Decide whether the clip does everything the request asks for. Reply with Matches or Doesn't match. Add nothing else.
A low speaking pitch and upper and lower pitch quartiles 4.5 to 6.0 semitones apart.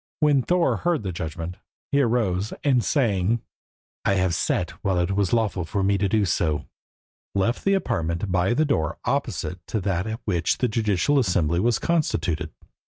Matches